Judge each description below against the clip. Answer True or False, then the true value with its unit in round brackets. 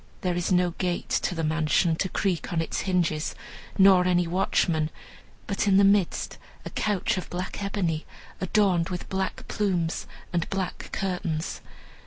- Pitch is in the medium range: True (180 Hz)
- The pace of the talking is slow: False (155 wpm)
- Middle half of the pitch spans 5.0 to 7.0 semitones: False (2.4 semitones)